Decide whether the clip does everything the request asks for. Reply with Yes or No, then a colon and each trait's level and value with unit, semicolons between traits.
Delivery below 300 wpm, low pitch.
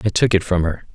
No: fast, 315 wpm; very low, 95 Hz